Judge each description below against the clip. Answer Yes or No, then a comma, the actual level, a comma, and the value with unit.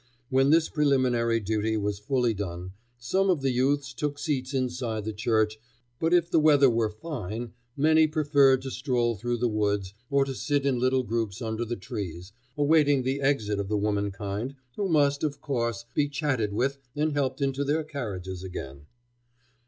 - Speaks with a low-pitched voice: Yes, low, 125 Hz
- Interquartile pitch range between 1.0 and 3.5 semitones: No, average, 4.9 semitones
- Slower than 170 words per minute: No, average, 175 wpm